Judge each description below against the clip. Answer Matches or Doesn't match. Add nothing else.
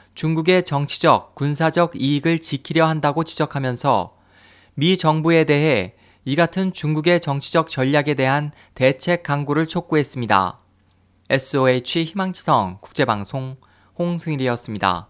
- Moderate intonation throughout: Matches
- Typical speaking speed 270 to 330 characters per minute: Matches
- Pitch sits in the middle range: Matches